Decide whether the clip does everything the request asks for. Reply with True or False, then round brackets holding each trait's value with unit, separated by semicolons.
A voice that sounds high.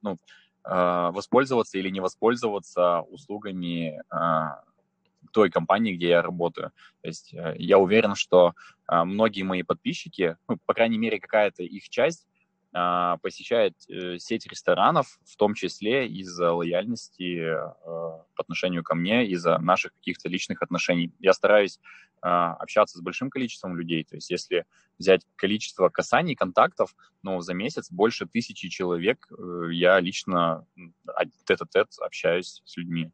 False (90 Hz)